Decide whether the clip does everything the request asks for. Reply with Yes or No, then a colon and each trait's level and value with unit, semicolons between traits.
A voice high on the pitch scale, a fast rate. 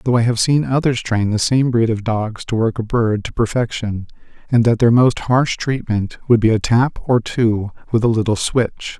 No: low, 115 Hz; fast, 220 wpm